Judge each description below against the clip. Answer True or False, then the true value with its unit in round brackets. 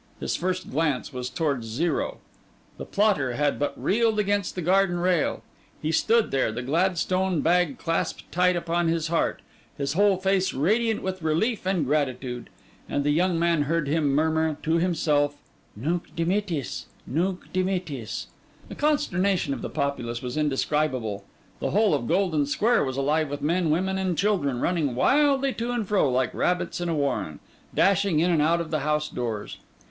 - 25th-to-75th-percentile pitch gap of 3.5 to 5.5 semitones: True (4.6 semitones)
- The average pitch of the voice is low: False (165 Hz)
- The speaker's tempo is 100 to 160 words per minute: False (170 wpm)